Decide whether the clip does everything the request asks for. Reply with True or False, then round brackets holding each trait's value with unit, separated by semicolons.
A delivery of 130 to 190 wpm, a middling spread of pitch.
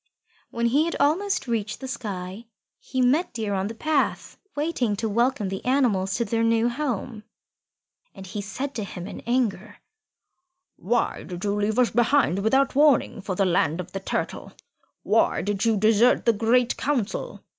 True (170 wpm; 4.2 semitones)